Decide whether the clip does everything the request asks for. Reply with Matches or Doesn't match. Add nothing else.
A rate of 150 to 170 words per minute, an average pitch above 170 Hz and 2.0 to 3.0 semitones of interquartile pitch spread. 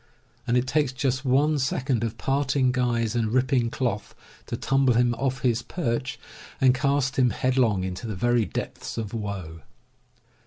Doesn't match